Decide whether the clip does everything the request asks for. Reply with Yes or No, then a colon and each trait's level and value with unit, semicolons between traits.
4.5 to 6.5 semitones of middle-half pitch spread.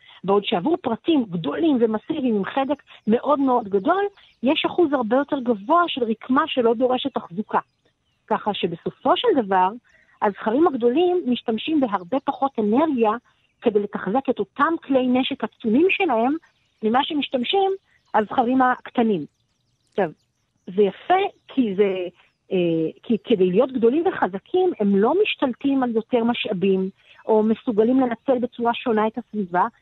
Yes: average, 5.0 semitones